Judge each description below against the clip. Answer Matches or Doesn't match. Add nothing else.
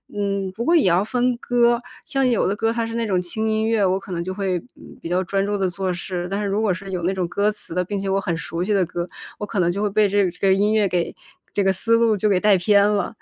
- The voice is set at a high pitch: Matches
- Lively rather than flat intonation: Doesn't match